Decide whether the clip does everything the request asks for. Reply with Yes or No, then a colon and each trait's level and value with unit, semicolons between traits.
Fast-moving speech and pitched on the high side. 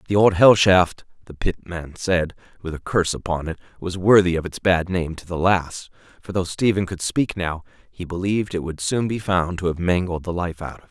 No: fast, 230 wpm; very low, 90 Hz